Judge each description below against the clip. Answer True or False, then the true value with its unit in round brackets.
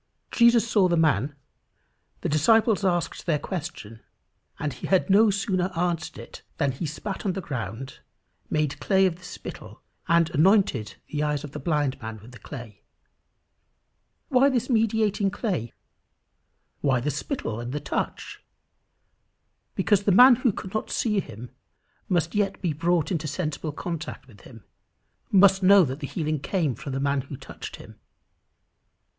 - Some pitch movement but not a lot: False (6.0 semitones)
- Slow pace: False (160 wpm)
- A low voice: False (170 Hz)